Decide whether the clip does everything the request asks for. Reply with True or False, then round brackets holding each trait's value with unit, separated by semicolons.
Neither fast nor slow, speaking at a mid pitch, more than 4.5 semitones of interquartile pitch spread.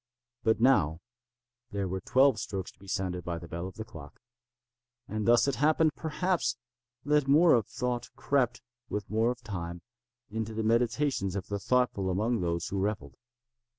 False (170 wpm; 110 Hz; 5.0 semitones)